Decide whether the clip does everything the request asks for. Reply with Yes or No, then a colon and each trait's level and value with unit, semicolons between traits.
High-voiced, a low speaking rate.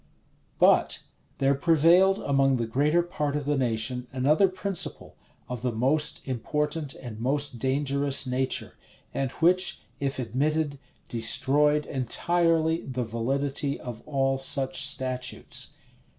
No: medium, 140 Hz; slow, 120 wpm